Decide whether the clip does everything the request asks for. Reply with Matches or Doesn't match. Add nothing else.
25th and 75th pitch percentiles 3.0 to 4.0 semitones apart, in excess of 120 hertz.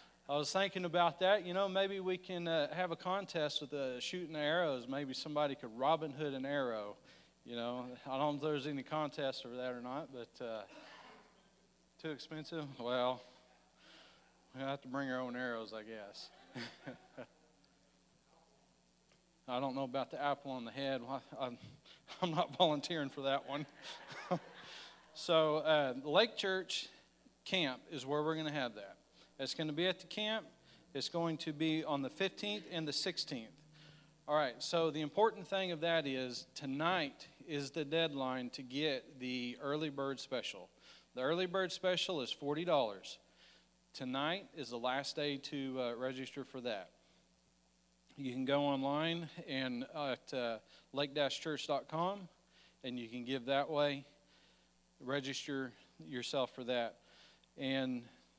Matches